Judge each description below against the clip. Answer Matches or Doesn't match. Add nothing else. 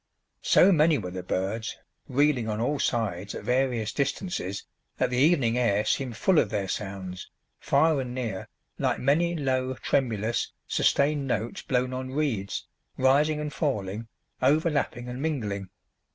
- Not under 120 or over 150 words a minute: Matches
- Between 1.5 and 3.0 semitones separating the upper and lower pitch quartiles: Doesn't match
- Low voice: Matches